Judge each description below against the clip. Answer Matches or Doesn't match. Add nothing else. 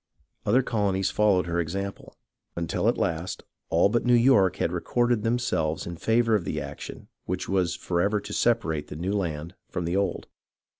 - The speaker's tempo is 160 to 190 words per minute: Matches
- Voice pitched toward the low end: Matches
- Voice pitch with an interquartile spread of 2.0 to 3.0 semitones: Doesn't match